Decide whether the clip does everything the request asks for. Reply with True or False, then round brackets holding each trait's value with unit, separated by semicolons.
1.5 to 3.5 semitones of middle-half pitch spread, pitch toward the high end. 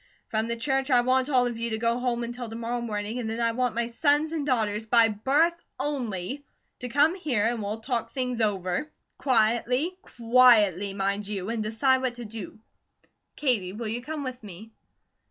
True (3.0 semitones; 235 Hz)